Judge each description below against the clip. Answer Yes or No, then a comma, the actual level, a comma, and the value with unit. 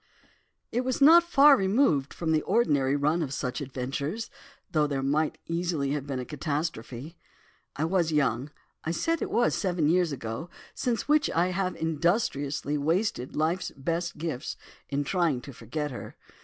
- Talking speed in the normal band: Yes, average, 160 wpm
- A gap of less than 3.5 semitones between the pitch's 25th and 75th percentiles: No, average, 4.5 semitones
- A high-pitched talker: No, medium, 155 Hz